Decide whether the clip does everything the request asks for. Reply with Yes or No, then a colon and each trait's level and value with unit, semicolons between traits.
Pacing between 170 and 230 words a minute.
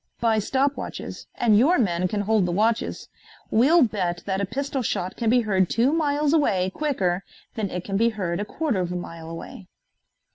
Yes: average, 195 wpm